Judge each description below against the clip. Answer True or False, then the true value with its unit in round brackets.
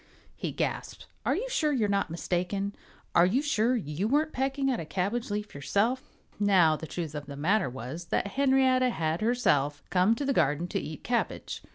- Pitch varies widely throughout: True (7.9 semitones)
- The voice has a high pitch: True (200 Hz)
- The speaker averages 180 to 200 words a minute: True (190 wpm)